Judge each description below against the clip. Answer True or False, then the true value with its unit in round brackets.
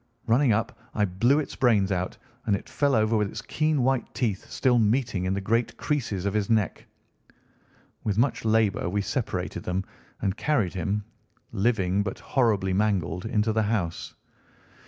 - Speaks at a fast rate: False (165 wpm)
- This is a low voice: True (105 Hz)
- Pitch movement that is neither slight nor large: True (3.6 semitones)